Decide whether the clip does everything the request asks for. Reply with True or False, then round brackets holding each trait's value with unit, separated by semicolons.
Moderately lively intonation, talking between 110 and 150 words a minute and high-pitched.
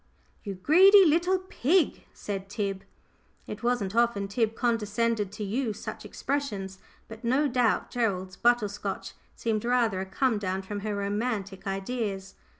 True (3.8 semitones; 145 wpm; 220 Hz)